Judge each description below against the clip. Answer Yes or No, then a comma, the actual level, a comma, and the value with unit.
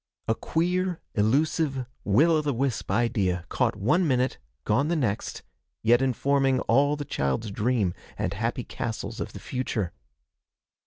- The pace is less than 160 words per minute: Yes, average, 145 wpm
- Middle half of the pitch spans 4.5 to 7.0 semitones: Yes, average, 5.1 semitones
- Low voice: Yes, low, 130 Hz